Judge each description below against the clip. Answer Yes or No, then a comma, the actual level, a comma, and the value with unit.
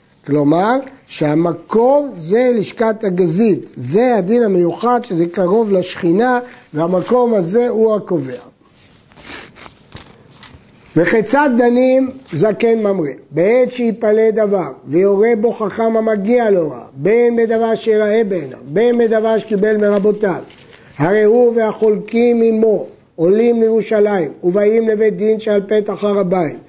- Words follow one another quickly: No, average, 110 wpm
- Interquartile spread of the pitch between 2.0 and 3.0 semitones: No, average, 3.7 semitones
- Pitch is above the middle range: Yes, high, 215 Hz